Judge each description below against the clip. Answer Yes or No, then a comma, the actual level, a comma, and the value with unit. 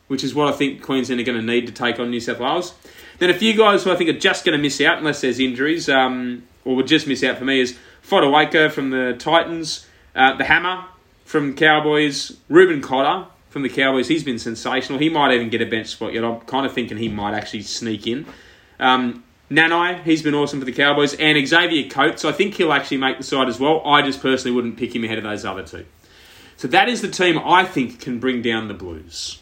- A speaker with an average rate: No, fast, 240 wpm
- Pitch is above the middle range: No, low, 135 Hz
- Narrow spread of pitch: No, average, 4.2 semitones